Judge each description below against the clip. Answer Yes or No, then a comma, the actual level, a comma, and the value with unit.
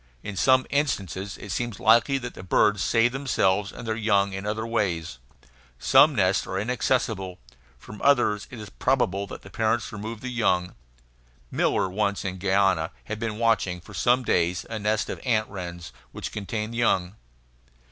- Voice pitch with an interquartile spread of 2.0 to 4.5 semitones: Yes, average, 3.4 semitones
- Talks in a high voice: No, low, 105 Hz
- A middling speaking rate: Yes, average, 165 wpm